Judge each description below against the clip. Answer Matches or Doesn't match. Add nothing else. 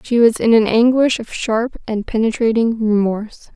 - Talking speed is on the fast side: Doesn't match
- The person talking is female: Matches